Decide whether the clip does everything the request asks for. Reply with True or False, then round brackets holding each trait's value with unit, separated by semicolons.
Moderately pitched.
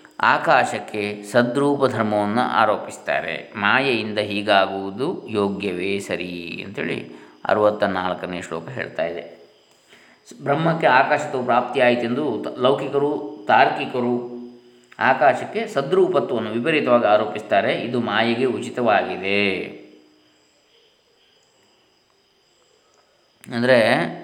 False (115 Hz)